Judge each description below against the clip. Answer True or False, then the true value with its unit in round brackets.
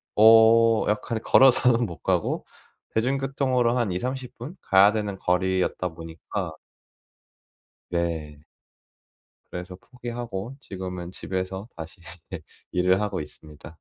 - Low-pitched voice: True (100 Hz)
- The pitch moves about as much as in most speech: True (4.8 semitones)